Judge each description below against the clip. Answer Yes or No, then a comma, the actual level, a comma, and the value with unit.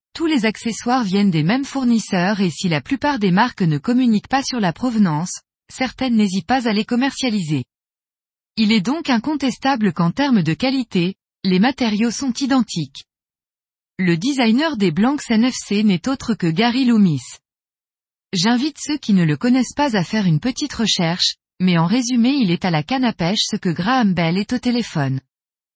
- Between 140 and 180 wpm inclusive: Yes, average, 175 wpm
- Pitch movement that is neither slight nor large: No, wide, 6.0 semitones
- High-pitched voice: Yes, high, 220 Hz